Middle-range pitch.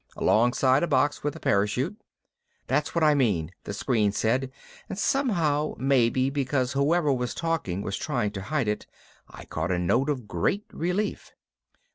No: low, 130 Hz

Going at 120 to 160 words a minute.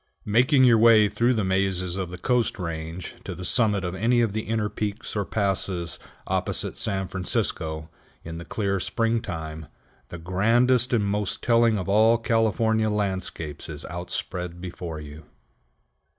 Yes: average, 150 wpm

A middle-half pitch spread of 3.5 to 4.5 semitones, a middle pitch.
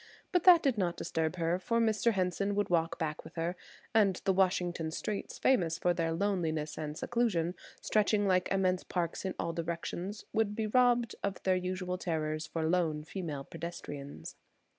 Yes: average, 3.8 semitones; medium, 180 Hz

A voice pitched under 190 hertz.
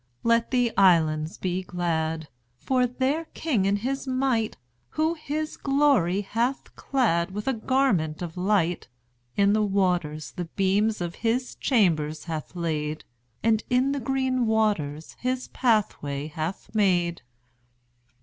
No: high, 205 Hz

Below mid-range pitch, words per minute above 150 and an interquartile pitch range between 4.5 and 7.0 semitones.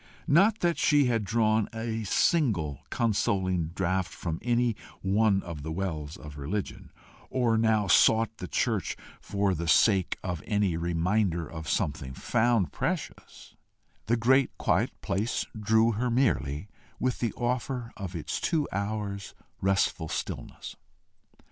No: low, 105 Hz; slow, 135 wpm; average, 5.0 semitones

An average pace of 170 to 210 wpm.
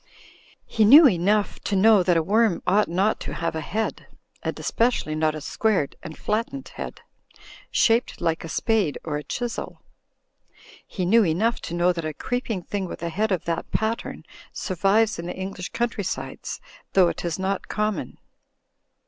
Yes: average, 175 wpm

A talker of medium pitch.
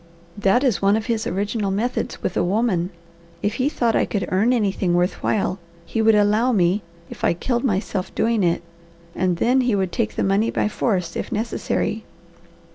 No: high, 210 Hz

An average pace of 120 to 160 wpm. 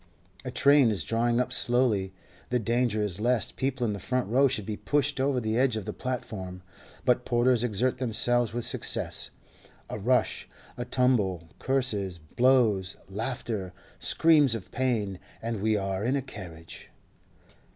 Yes: average, 150 wpm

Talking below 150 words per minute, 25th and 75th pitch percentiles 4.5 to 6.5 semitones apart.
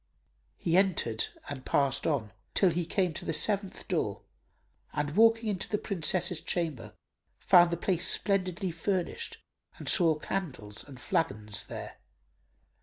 Yes: average, 140 wpm; average, 4.9 semitones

